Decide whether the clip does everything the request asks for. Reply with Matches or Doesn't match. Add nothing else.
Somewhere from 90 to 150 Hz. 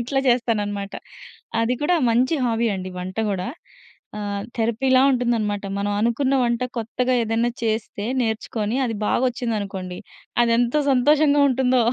Doesn't match